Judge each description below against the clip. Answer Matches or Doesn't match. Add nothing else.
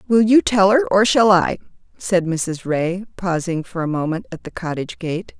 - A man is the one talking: Doesn't match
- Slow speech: Doesn't match